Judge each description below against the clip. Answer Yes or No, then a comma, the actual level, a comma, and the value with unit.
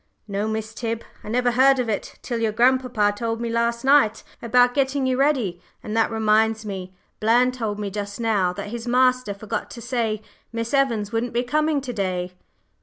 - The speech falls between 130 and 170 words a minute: No, average, 190 wpm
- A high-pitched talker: Yes, high, 230 Hz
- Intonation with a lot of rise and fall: No, average, 2.9 semitones